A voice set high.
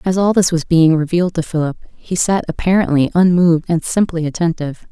No: medium, 170 Hz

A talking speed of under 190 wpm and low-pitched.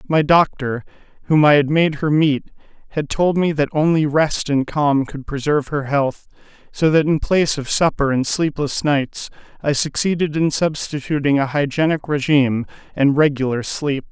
No: average, 165 wpm; medium, 145 Hz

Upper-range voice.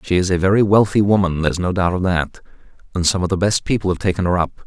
No: very low, 95 Hz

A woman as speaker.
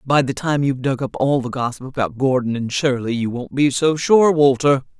Yes: female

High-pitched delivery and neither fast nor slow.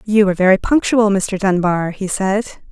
Yes: high, 195 Hz; average, 175 wpm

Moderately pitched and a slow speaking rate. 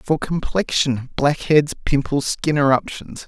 Yes: medium, 145 Hz; slow, 110 wpm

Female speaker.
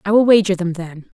Yes: female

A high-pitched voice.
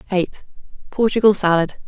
Yes: high, 195 Hz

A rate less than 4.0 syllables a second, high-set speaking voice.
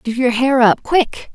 Yes: 3.8 syllables/s; very high, 250 Hz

